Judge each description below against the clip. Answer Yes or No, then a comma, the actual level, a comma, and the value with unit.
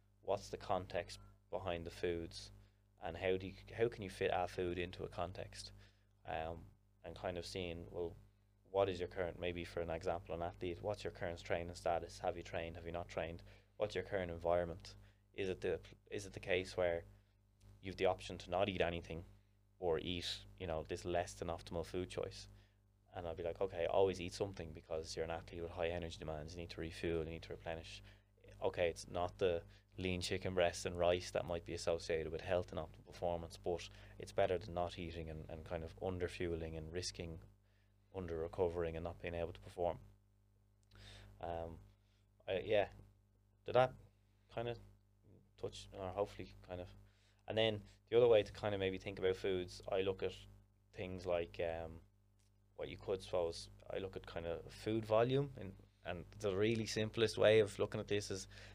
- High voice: No, very low, 95 Hz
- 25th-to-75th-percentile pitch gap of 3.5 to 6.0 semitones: No, average, 2.9 semitones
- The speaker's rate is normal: Yes, average, 195 wpm